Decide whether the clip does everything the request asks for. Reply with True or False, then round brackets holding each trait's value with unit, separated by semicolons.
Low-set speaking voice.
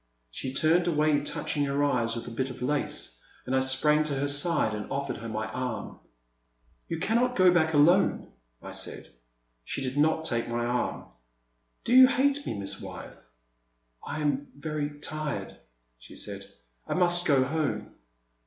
False (145 Hz)